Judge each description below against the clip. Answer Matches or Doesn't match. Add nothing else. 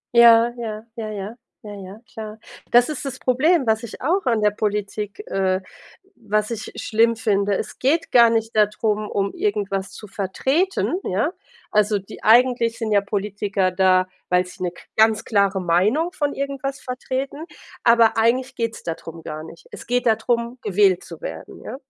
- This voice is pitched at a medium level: Doesn't match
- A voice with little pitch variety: Doesn't match